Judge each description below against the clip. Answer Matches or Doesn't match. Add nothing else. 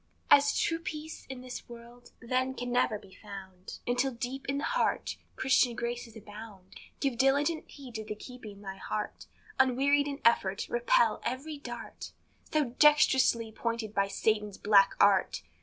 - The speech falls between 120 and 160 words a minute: Matches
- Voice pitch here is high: Matches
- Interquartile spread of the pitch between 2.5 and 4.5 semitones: Matches